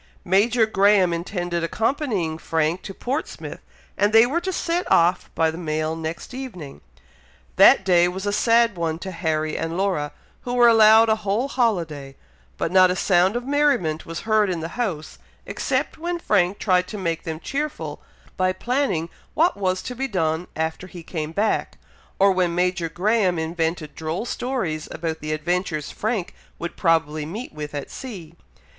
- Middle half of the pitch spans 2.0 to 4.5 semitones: No, average, 5.3 semitones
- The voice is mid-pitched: Yes, medium, 180 Hz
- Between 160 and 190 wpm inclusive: Yes, average, 170 wpm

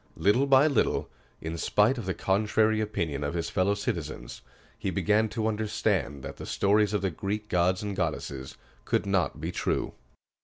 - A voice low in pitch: Yes, low, 100 Hz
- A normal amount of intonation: Yes, average, 3.8 semitones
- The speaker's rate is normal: Yes, average, 170 wpm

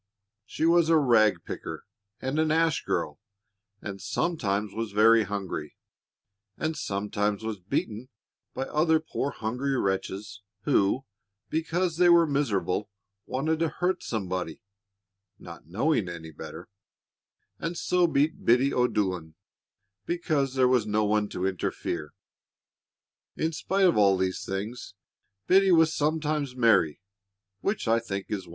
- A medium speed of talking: No, slow, 130 wpm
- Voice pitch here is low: Yes, low, 120 Hz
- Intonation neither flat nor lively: No, wide, 7.9 semitones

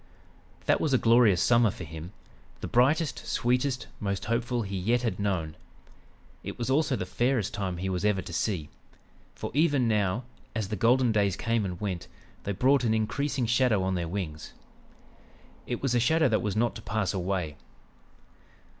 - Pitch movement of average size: Yes, average, 4.6 semitones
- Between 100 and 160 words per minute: No, average, 175 wpm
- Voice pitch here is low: Yes, low, 110 Hz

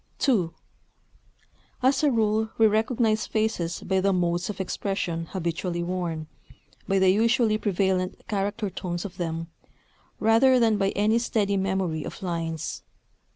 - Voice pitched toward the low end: No, high, 195 Hz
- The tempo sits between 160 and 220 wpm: No, slow, 135 wpm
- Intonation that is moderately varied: Yes, average, 3.8 semitones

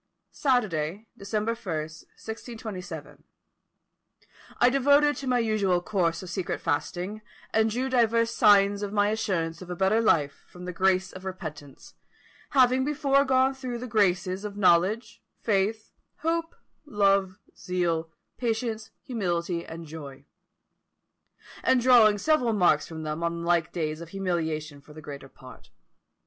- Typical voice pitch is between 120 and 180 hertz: No, high, 195 Hz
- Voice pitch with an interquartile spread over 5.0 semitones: Yes, wide, 5.4 semitones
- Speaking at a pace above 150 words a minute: No, slow, 135 wpm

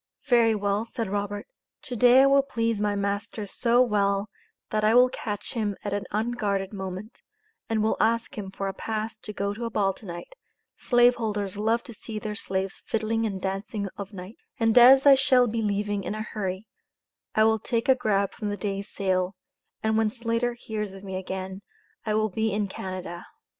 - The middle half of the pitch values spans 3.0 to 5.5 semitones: No, narrow, 2.5 semitones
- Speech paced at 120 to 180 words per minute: No, average, 200 wpm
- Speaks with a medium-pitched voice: No, high, 210 Hz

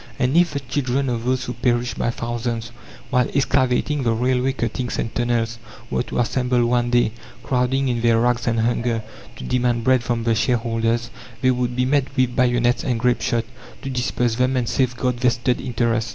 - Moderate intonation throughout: No, narrow, 1.5 semitones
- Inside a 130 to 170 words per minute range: No, average, 180 wpm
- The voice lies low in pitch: Yes, low, 120 Hz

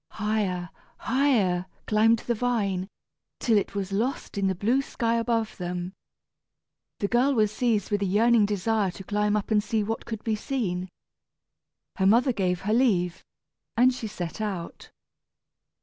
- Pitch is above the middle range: Yes, high, 210 Hz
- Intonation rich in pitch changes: No, average, 3.2 semitones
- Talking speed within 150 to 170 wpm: Yes, average, 155 wpm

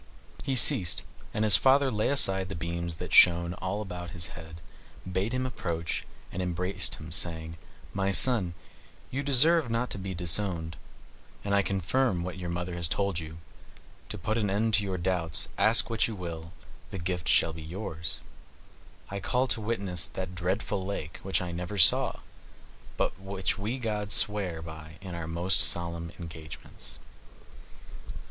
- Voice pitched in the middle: No, very low, 95 Hz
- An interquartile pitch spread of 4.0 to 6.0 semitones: No, average, 3.5 semitones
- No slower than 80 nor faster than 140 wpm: No, average, 165 wpm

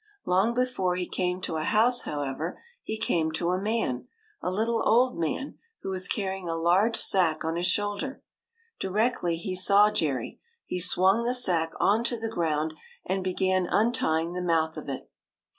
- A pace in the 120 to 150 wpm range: No, average, 175 wpm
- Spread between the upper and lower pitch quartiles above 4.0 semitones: Yes, average, 4.6 semitones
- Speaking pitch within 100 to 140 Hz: No, medium, 185 Hz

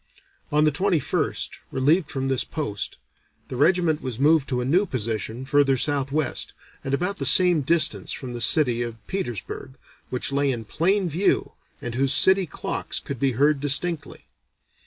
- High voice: No, medium, 140 Hz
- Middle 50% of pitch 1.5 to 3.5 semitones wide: No, average, 4.1 semitones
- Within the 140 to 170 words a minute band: Yes, average, 160 wpm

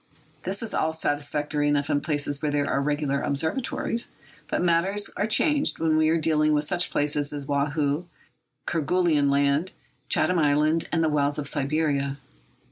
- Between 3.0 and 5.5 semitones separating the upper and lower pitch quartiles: No, narrow, 2.4 semitones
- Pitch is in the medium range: Yes, medium, 150 Hz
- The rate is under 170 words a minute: Yes, average, 160 wpm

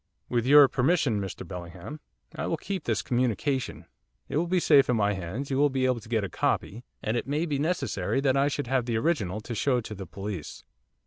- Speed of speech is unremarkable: No, fast, 220 wpm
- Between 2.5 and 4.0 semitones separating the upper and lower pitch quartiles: No, average, 5.2 semitones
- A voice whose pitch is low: Yes, low, 125 Hz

